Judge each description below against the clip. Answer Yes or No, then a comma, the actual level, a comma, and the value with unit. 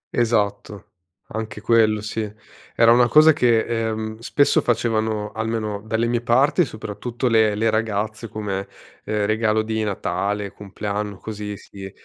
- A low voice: Yes, low, 110 Hz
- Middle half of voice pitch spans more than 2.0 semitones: No, narrow, 1.7 semitones